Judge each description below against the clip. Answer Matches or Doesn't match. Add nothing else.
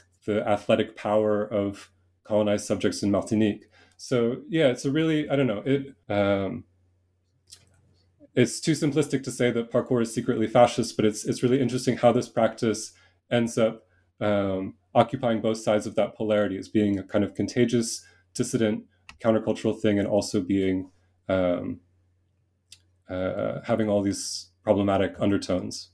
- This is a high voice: Doesn't match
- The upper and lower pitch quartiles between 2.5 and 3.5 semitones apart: Doesn't match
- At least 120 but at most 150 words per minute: Matches